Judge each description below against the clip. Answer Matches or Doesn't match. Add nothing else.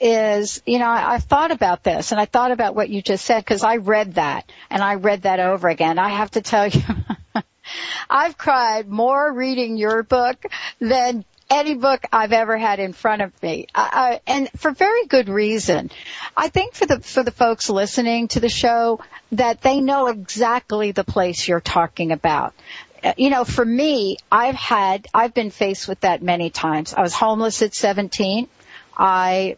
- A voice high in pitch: Matches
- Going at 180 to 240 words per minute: Matches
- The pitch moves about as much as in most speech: Matches